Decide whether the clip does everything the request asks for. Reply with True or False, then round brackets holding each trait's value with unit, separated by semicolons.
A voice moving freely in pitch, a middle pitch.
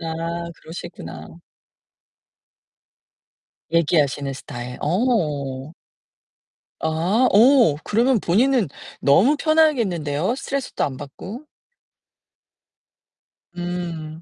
True (8.3 semitones; 175 Hz)